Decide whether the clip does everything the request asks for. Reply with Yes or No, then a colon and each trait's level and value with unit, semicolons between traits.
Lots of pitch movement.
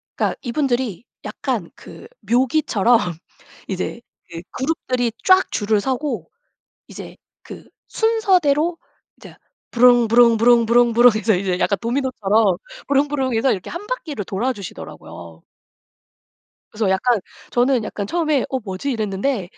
No: average, 4.5 semitones